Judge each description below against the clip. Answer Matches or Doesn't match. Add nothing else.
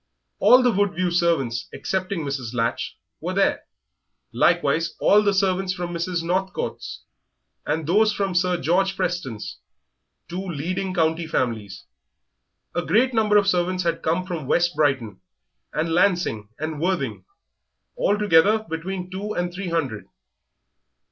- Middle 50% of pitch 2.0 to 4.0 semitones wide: Matches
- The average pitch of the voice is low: Doesn't match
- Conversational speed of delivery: Doesn't match